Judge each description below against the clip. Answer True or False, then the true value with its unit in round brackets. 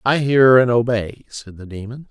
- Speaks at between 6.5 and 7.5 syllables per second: False (4.6 syllables/s)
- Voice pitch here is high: False (120 Hz)